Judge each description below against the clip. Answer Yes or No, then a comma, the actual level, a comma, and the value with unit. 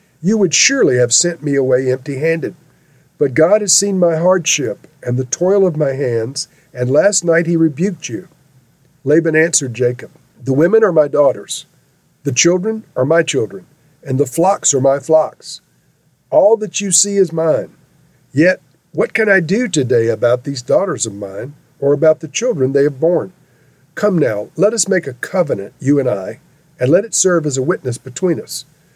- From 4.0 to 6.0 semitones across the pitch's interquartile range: Yes, average, 4.8 semitones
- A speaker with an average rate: Yes, average, 180 wpm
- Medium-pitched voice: Yes, medium, 155 Hz